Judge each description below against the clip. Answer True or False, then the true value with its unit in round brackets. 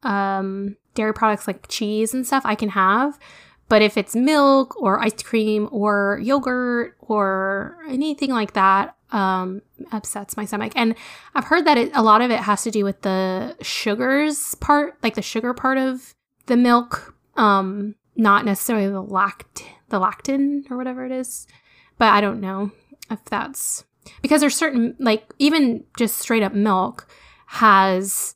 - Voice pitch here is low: False (225 Hz)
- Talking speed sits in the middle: True (165 wpm)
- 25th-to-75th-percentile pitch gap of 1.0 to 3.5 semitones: False (4.3 semitones)